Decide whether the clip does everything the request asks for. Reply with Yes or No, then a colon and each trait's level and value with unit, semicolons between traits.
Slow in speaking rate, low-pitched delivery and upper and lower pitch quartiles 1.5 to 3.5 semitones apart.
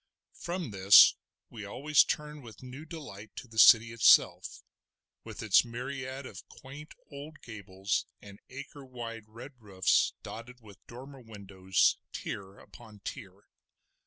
No: slow, 130 wpm; low, 115 Hz; average, 5.1 semitones